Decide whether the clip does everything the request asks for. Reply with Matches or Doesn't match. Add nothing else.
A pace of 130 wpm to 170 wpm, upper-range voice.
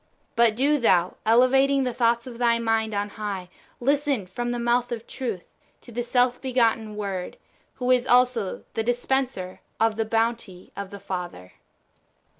Matches